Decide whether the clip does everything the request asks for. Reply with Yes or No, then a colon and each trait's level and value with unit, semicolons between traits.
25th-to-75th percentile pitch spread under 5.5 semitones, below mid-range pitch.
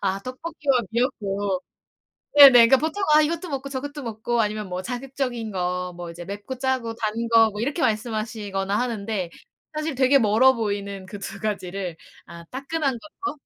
No: average, 5.1 semitones; high, 225 Hz